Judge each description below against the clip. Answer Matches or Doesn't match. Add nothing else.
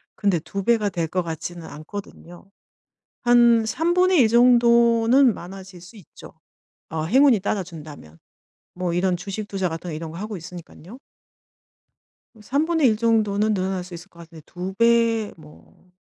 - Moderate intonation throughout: Matches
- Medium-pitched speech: Doesn't match